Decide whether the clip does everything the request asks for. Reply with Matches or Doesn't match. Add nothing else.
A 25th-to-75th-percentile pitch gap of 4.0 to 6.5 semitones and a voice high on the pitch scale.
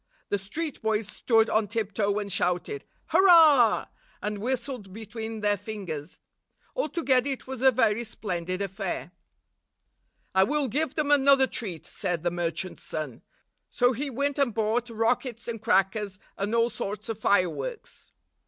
Matches